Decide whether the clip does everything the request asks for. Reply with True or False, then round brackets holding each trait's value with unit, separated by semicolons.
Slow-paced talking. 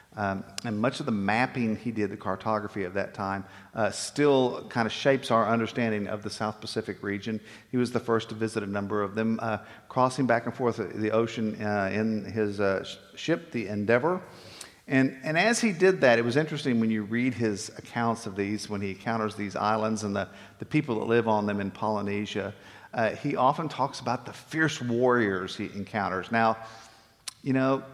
False (200 wpm)